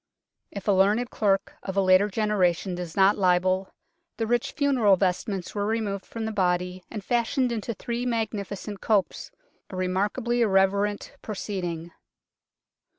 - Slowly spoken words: No, average, 145 wpm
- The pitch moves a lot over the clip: No, average, 3.0 semitones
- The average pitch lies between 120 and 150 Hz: No, high, 200 Hz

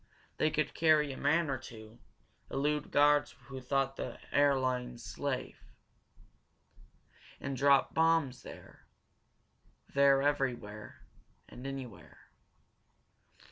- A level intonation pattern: Yes, narrow, 2.3 semitones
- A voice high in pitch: No, low, 135 Hz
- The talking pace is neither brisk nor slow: No, slow, 100 wpm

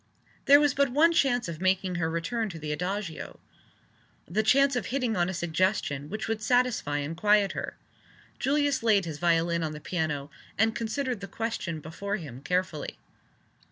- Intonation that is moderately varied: No, wide, 6.1 semitones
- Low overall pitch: No, high, 190 Hz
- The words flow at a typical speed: Yes, average, 170 wpm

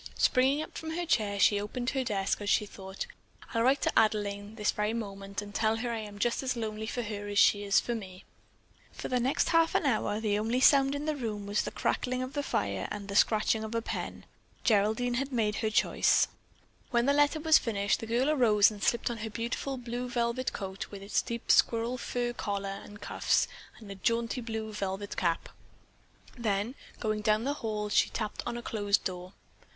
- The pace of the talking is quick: Yes, fast, 210 wpm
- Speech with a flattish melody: No, average, 3.2 semitones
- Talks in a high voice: Yes, high, 220 Hz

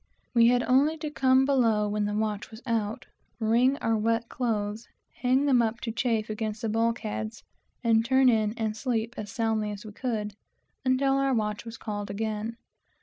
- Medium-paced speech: Yes, average, 160 wpm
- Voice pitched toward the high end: Yes, high, 225 Hz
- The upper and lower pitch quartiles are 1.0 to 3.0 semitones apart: Yes, average, 2.7 semitones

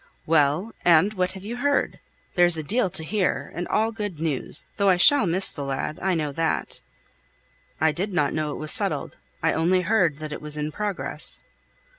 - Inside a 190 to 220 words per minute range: Yes, average, 195 wpm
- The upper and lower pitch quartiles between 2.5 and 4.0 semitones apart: No, average, 4.5 semitones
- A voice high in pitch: No, medium, 175 Hz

